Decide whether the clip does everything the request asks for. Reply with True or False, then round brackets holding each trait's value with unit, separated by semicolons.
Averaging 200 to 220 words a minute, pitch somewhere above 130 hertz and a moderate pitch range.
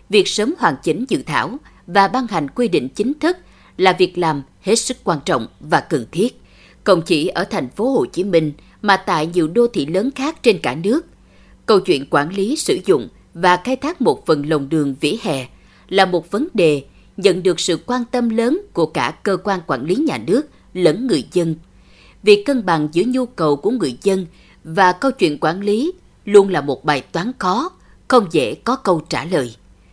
False (205 wpm; 190 Hz; 7.4 semitones)